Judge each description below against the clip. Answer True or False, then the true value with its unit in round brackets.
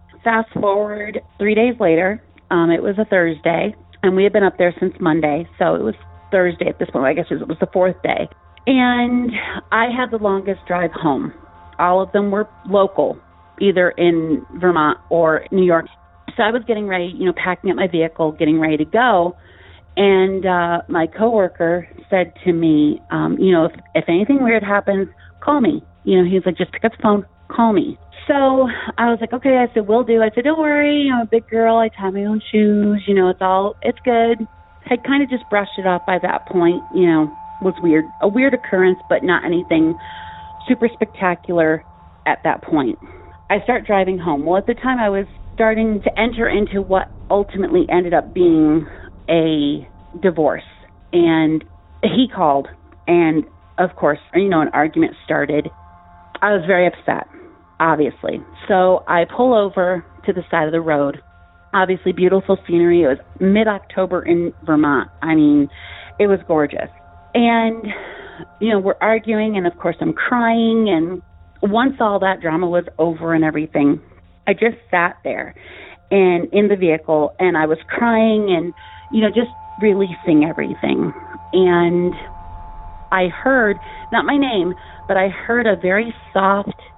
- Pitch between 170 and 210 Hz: True (185 Hz)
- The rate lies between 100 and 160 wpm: False (175 wpm)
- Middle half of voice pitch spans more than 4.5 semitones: True (5.1 semitones)